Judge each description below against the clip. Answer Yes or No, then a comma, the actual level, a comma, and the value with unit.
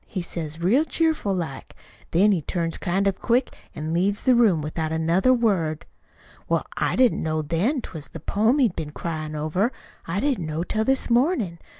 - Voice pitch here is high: No, medium, 180 Hz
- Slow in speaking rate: No, average, 190 wpm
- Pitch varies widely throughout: Yes, wide, 6.6 semitones